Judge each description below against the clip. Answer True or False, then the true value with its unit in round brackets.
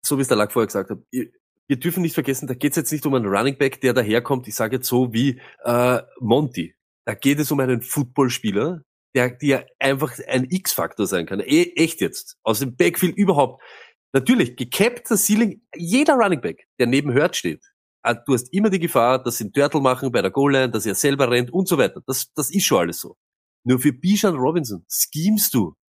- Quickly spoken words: True (215 wpm)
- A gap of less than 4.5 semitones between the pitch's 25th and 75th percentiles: False (5.5 semitones)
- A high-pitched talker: False (140 Hz)